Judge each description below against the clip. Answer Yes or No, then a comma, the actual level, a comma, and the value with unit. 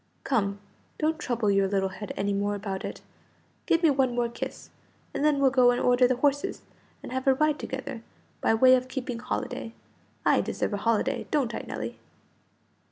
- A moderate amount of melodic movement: Yes, average, 4.0 semitones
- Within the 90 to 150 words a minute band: No, average, 185 wpm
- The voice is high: Yes, very high, 250 Hz